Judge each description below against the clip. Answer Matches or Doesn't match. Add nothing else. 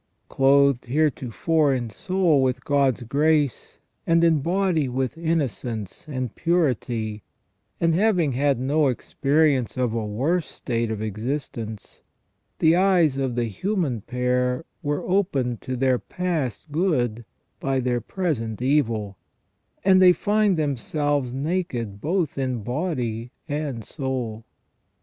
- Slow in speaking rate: Matches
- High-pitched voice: Doesn't match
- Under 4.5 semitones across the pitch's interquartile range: Doesn't match